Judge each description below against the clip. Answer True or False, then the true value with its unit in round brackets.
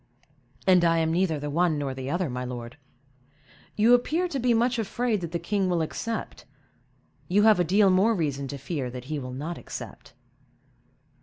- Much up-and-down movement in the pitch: True (6.6 semitones)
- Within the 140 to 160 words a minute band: False (185 wpm)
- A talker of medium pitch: True (170 Hz)